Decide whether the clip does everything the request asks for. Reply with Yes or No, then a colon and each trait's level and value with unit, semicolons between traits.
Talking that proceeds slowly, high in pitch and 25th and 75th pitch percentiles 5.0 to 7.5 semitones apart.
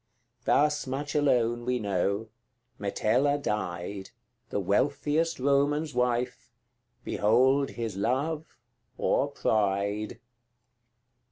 No: slow, 85 wpm; low, 125 Hz; wide, 5.5 semitones